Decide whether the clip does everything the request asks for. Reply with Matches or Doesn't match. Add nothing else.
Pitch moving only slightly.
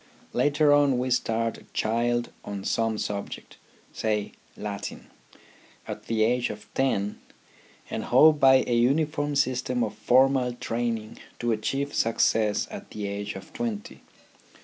Doesn't match